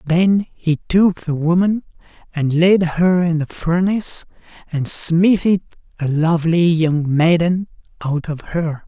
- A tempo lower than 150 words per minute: Yes, slow, 135 wpm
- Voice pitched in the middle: Yes, medium, 170 Hz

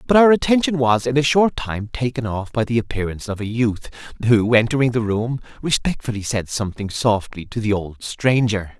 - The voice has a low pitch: Yes, low, 120 Hz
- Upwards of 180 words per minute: Yes, average, 190 wpm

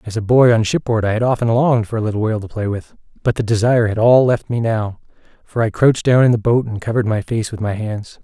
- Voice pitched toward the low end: Yes, low, 115 Hz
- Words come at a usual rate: No, fast, 275 wpm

